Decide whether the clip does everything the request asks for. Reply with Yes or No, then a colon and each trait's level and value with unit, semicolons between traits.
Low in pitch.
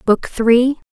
No: high, 240 Hz